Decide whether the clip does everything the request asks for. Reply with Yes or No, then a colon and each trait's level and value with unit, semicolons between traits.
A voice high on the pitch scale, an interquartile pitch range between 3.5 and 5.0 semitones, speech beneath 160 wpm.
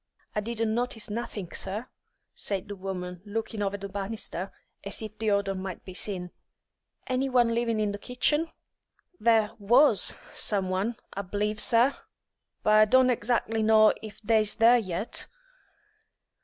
No: high, 215 Hz; narrow, 2.6 semitones; average, 150 wpm